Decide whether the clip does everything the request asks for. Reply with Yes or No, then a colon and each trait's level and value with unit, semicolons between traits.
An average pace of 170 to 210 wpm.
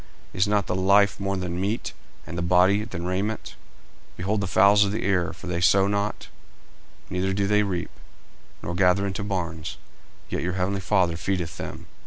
Yes: average, 185 wpm